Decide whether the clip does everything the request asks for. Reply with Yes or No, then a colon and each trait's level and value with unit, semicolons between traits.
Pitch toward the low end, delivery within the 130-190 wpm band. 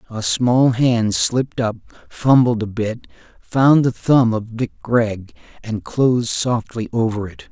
Yes: low, 115 Hz; average, 150 wpm